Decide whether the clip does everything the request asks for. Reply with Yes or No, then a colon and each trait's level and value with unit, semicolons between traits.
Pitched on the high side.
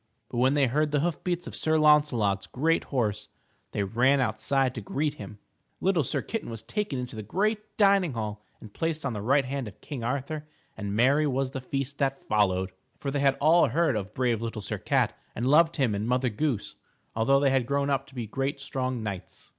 No: low, 135 Hz